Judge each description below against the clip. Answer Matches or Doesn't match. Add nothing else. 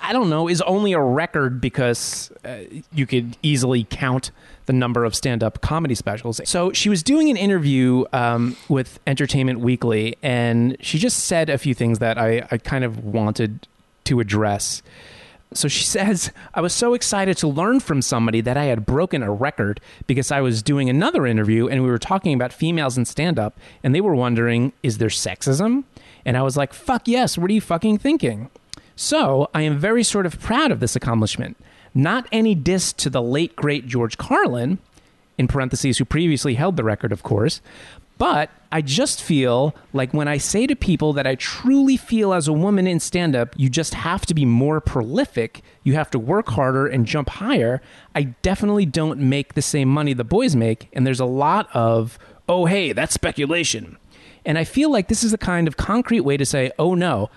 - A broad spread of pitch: Matches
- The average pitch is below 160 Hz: Matches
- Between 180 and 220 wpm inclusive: Matches